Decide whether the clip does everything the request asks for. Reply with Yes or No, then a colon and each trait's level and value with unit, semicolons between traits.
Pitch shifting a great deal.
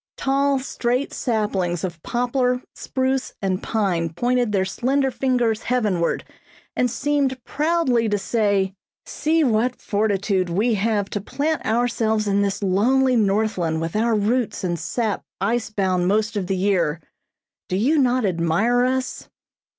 No: average, 4.5 semitones